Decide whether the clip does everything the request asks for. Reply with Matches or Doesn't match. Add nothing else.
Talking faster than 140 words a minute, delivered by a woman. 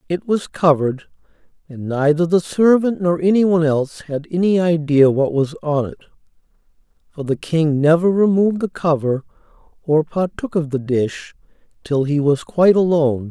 Doesn't match